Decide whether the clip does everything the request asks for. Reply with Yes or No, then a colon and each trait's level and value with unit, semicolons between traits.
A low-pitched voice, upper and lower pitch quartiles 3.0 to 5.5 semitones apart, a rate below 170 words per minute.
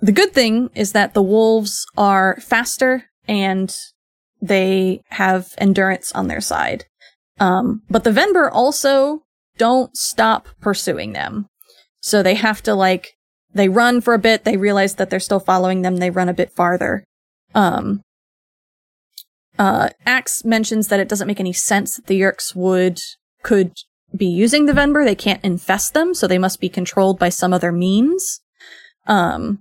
No: high, 205 Hz; average, 4.0 semitones; average, 160 wpm